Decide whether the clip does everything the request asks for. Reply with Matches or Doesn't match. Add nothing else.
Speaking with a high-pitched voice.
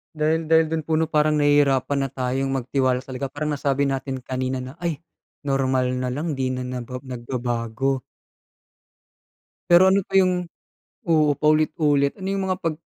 Doesn't match